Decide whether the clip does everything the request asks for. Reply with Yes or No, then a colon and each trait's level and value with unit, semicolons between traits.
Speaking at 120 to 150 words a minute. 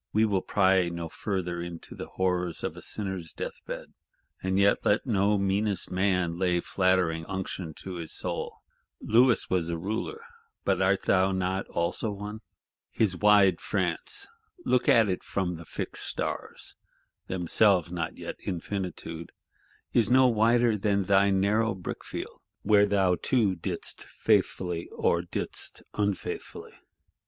Yes: average, 140 wpm